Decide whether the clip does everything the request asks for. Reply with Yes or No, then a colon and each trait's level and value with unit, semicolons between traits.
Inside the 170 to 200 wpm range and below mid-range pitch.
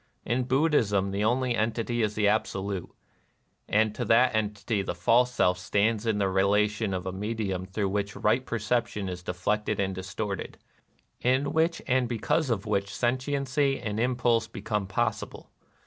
Yes: average, 175 wpm; low, 110 Hz